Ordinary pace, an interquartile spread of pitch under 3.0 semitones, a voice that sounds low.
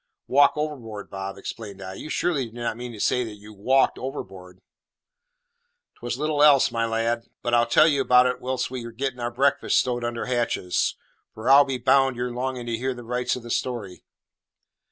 Yes: average, 195 wpm; narrow, 2.4 semitones; low, 120 Hz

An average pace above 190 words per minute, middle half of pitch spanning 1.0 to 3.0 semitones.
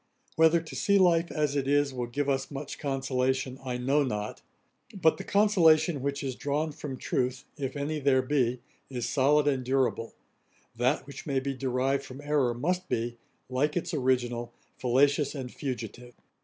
No: average, 170 wpm; average, 2.7 semitones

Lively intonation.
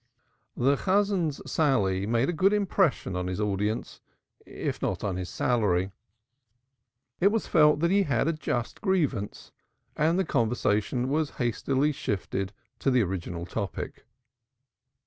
Yes: wide, 8.0 semitones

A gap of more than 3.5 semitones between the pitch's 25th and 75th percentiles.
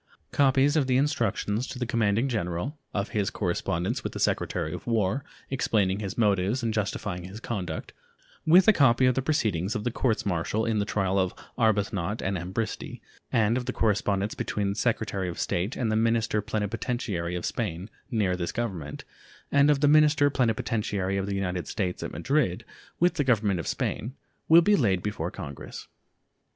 Yes: average, 4.8 semitones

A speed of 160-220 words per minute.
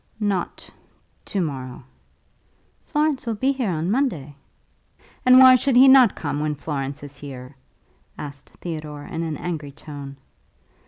No: average, 140 wpm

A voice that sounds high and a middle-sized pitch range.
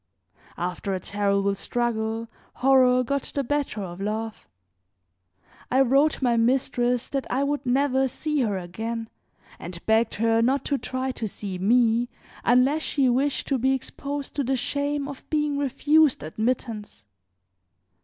Yes: very high, 250 Hz; average, 3.9 semitones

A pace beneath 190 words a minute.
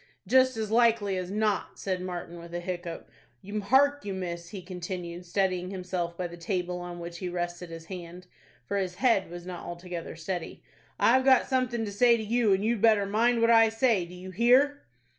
No: average, 200 wpm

